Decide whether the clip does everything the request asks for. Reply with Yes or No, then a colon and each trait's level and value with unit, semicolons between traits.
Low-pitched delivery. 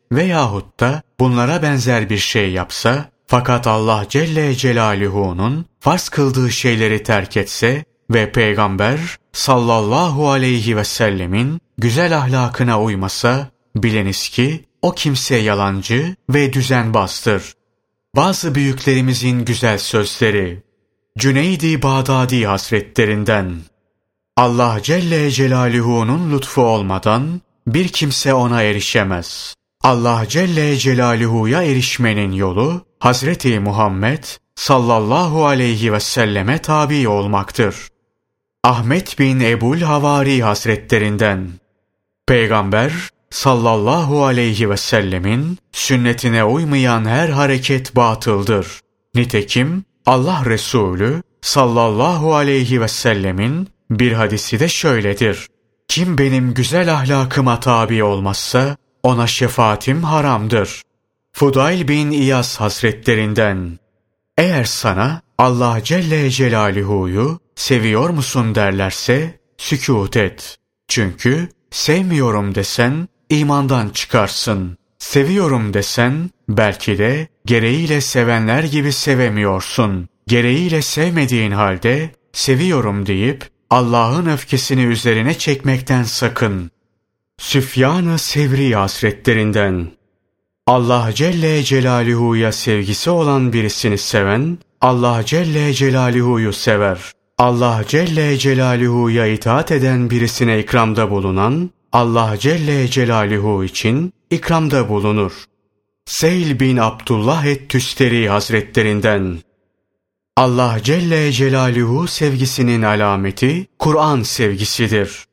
Yes: low, 120 Hz